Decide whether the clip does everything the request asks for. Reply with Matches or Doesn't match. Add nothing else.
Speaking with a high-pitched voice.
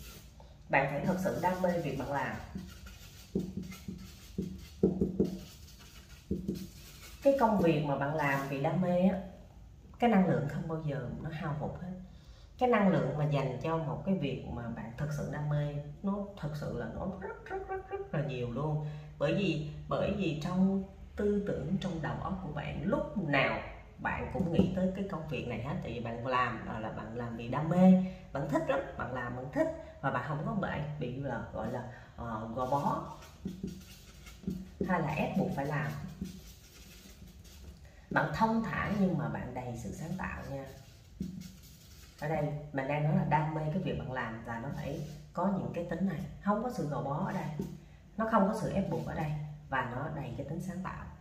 Doesn't match